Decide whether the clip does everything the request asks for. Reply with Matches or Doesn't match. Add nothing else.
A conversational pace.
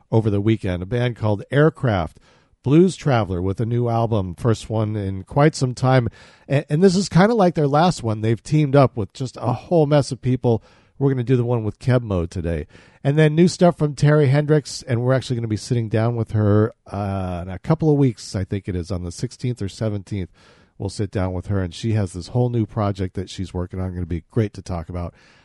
Doesn't match